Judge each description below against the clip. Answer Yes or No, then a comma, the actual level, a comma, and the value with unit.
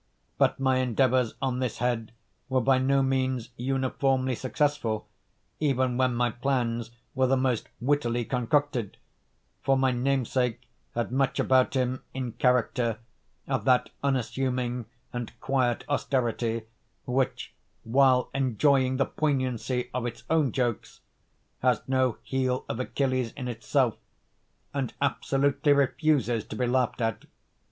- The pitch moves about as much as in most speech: No, narrow, 1.7 semitones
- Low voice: Yes, low, 130 Hz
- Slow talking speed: Yes, slow, 130 wpm